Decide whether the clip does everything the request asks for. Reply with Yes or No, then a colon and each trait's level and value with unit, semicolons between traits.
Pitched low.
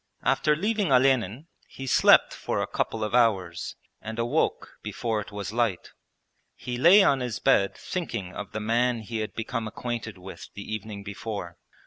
Yes: low, 115 Hz